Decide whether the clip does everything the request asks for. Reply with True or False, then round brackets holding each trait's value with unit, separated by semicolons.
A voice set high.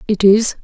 True (205 Hz)